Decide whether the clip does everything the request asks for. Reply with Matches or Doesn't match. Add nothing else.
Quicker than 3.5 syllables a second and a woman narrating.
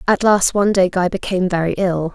Matches